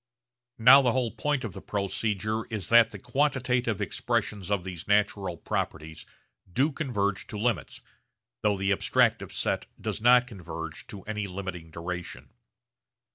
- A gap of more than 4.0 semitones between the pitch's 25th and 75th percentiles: Yes, average, 4.6 semitones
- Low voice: Yes, low, 105 Hz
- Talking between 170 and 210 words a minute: No, average, 140 wpm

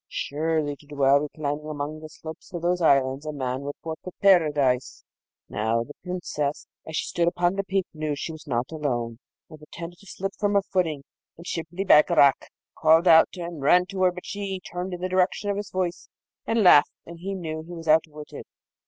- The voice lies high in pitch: No, medium, 160 Hz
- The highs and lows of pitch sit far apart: No, average, 3.5 semitones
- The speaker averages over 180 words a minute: Yes, average, 200 wpm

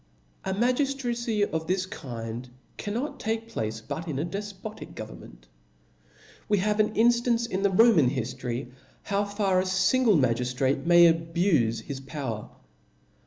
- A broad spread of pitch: Yes, wide, 8.5 semitones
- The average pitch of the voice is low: No, medium, 185 Hz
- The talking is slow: Yes, slow, 130 wpm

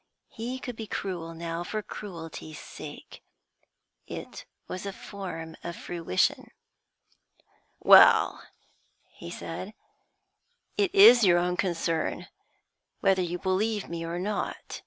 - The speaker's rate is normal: No, slow, 115 wpm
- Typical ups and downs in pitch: Yes, average, 3.8 semitones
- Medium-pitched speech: Yes, medium, 180 Hz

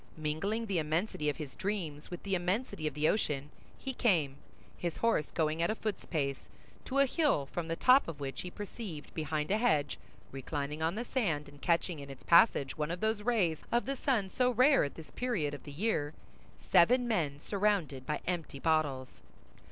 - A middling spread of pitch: No, wide, 6.4 semitones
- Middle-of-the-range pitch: Yes, medium, 165 Hz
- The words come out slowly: No, average, 195 wpm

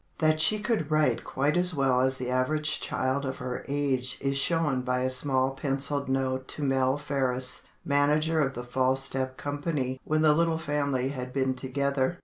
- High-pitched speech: No, low, 135 Hz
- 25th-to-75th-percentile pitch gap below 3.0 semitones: Yes, narrow, 2.4 semitones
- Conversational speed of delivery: Yes, average, 180 wpm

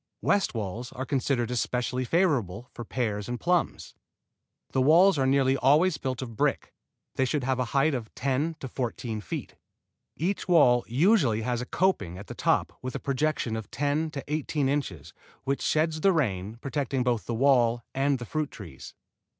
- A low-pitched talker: Yes, low, 130 Hz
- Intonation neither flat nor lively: Yes, average, 3.9 semitones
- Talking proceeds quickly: No, average, 175 wpm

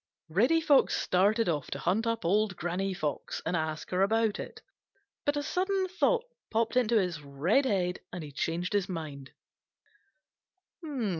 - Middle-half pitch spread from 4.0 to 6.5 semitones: Yes, wide, 5.5 semitones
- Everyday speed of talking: Yes, average, 155 wpm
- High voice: Yes, high, 195 Hz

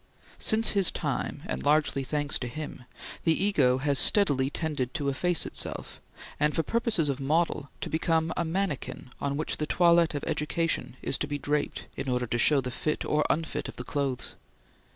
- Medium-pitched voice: Yes, medium, 150 Hz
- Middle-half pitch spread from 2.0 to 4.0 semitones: Yes, average, 3.2 semitones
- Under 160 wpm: No, average, 185 wpm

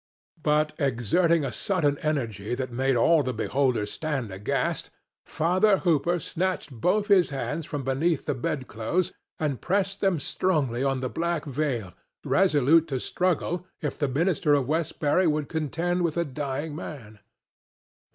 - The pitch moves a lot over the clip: No, average, 4.4 semitones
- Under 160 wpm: Yes, average, 145 wpm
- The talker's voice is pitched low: No, medium, 150 Hz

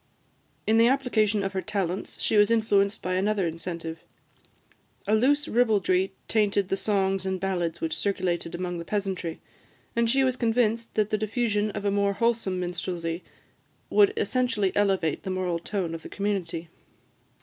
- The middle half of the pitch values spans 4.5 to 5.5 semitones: No, average, 3.2 semitones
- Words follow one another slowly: No, average, 160 wpm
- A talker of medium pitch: No, high, 200 Hz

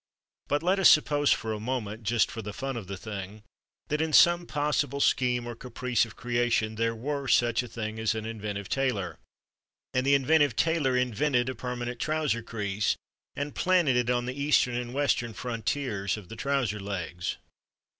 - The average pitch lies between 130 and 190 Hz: No, low, 120 Hz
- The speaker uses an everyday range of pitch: Yes, average, 4.2 semitones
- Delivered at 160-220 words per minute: Yes, average, 180 wpm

